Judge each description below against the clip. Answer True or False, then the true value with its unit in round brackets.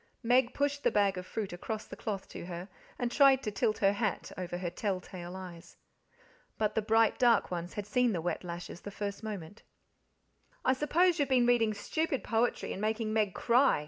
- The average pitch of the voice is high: True (215 Hz)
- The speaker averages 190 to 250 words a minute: True (200 wpm)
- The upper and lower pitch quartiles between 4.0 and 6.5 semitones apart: True (4.6 semitones)